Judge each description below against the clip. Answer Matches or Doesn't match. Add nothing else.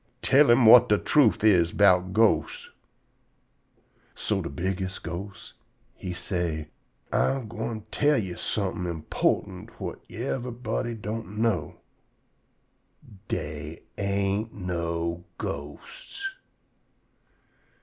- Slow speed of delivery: Matches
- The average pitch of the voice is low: Matches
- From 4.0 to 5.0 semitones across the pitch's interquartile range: Matches